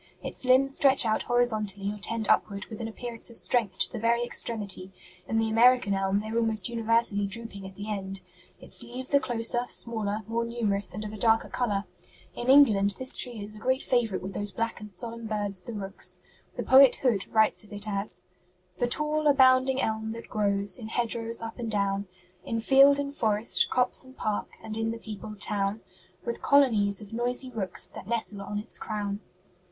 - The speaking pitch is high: Yes, high, 225 Hz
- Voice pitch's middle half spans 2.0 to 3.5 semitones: Yes, average, 2.9 semitones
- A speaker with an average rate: Yes, average, 195 wpm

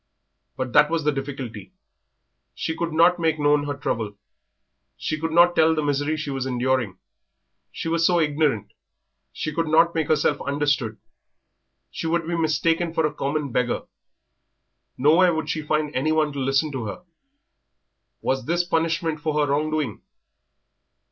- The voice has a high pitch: No, medium, 150 Hz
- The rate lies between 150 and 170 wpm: Yes, average, 155 wpm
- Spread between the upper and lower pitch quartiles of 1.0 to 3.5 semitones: Yes, average, 2.9 semitones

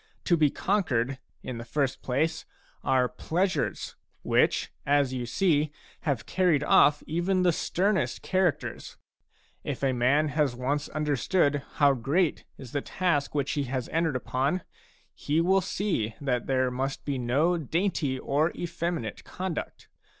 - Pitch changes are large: No, average, 4.6 semitones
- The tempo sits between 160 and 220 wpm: No, average, 145 wpm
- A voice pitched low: No, medium, 145 Hz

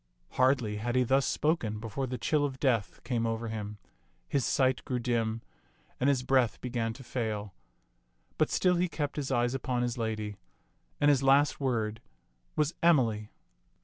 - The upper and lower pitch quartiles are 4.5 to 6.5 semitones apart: No, average, 3.3 semitones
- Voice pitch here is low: Yes, low, 125 Hz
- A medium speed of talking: Yes, average, 165 wpm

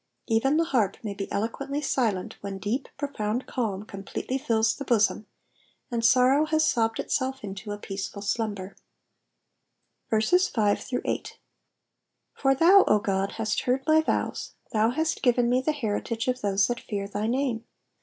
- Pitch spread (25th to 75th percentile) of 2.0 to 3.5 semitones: No, average, 4.6 semitones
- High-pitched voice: Yes, high, 230 Hz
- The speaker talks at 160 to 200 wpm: No, average, 150 wpm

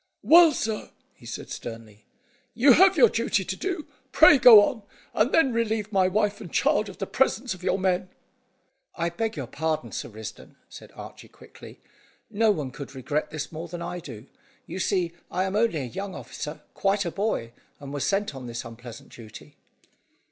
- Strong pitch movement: Yes, wide, 7.3 semitones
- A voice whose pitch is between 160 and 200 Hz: Yes, high, 190 Hz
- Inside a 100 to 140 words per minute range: No, average, 185 wpm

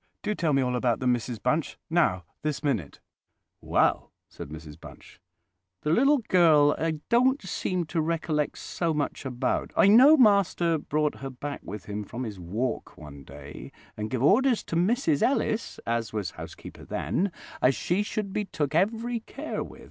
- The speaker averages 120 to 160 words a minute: No, average, 170 wpm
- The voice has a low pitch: No, medium, 150 Hz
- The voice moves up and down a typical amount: No, wide, 8.4 semitones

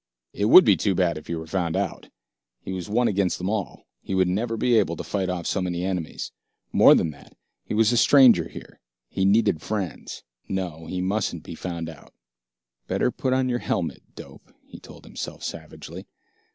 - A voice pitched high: No, very low, 95 Hz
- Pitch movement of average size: Yes, average, 4.1 semitones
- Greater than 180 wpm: Yes, average, 195 wpm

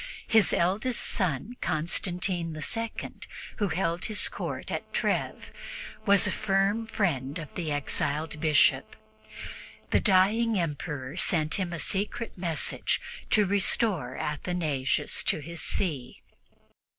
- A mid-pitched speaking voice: Yes, medium, 175 Hz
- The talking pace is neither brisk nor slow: No, slow, 115 wpm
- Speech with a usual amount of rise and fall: Yes, average, 4.7 semitones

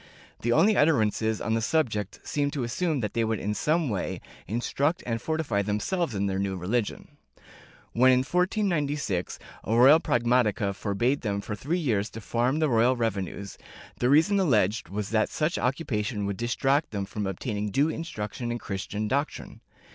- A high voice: No, low, 120 Hz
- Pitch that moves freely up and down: Yes, wide, 5.7 semitones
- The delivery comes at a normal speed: Yes, average, 175 wpm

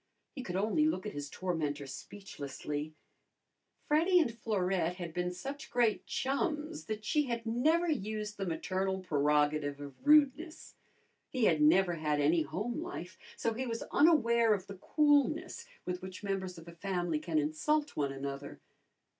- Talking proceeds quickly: No, average, 155 wpm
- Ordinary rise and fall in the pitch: No, wide, 8.7 semitones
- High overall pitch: Yes, high, 195 Hz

